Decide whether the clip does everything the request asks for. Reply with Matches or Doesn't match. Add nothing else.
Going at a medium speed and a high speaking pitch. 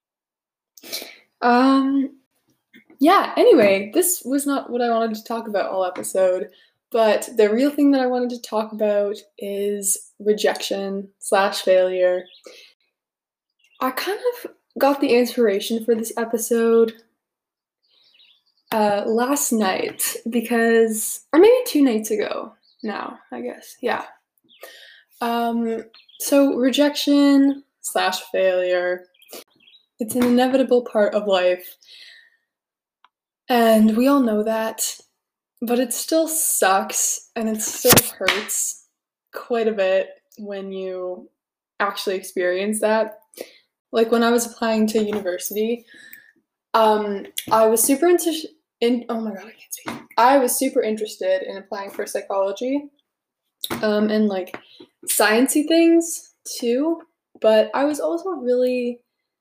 Doesn't match